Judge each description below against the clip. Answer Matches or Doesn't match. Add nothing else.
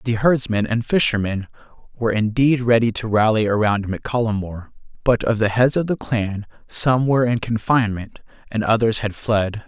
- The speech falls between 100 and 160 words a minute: Doesn't match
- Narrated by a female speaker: Doesn't match